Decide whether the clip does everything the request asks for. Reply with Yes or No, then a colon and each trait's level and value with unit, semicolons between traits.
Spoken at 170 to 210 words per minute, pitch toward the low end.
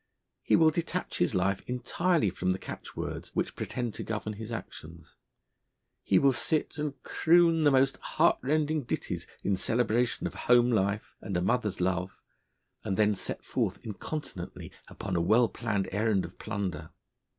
No: average, 155 wpm; low, 110 Hz